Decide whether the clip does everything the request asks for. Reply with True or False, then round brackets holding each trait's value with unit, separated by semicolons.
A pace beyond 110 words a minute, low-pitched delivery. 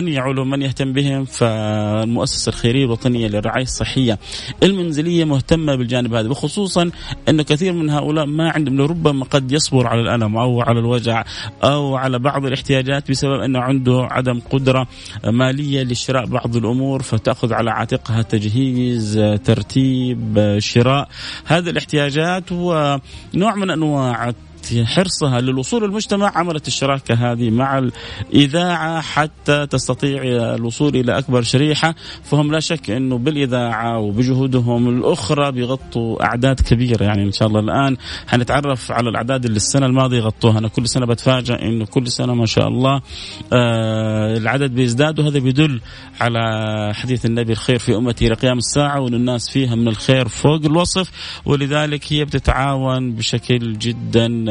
True (135 wpm; 130 Hz)